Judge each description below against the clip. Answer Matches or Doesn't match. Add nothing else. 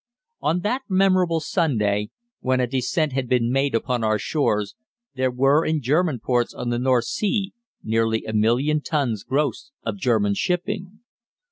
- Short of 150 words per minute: Doesn't match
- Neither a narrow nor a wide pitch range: Doesn't match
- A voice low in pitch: Matches